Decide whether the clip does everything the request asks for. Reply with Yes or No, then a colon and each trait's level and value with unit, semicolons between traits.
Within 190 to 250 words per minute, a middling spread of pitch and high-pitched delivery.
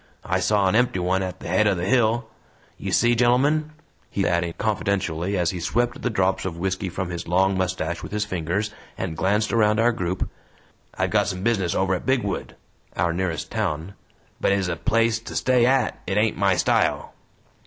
No: average, 195 wpm; average, 3.8 semitones; very low, 95 Hz